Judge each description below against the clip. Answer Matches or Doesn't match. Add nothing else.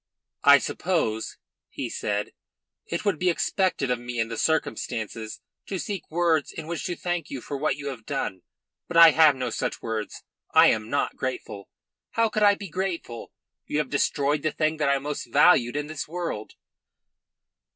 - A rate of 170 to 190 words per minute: Matches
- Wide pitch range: Matches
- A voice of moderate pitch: Matches